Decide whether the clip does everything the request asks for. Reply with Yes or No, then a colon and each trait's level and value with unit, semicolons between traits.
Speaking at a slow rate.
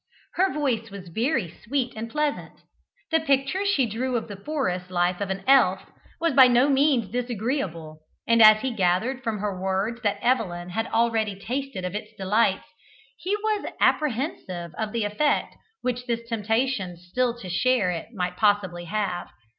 No: average, 165 wpm